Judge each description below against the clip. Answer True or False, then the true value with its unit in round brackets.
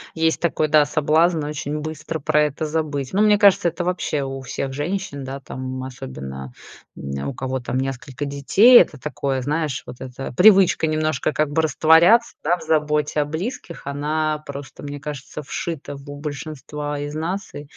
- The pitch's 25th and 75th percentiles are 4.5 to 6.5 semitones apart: False (2.8 semitones)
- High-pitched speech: False (150 Hz)